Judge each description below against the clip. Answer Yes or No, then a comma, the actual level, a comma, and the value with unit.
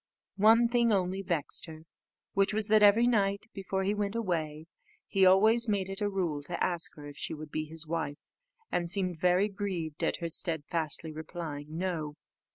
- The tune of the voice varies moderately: Yes, average, 4.2 semitones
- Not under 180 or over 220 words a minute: Yes, average, 185 wpm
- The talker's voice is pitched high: No, medium, 180 Hz